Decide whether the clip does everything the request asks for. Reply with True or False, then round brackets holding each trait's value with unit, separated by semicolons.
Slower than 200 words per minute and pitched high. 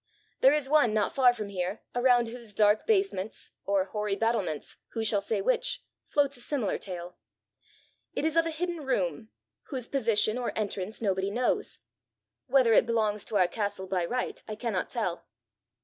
True (170 wpm; 220 Hz)